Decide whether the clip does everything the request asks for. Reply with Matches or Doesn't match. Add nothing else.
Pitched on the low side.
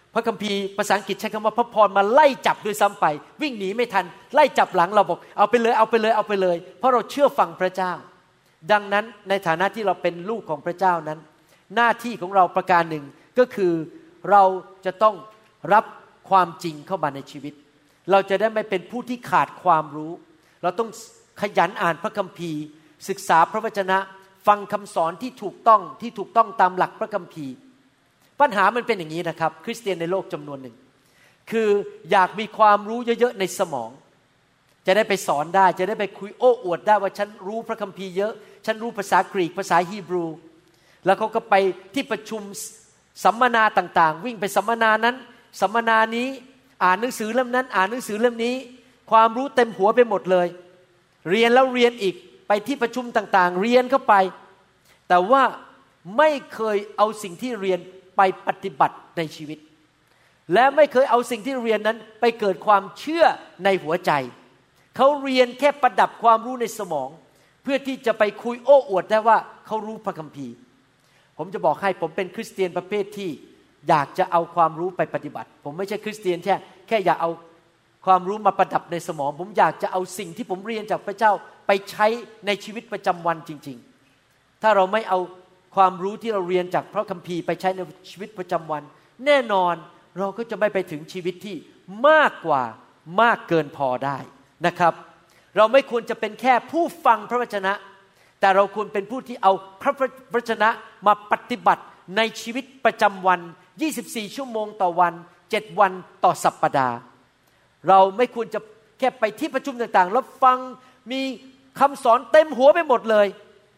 Doesn't match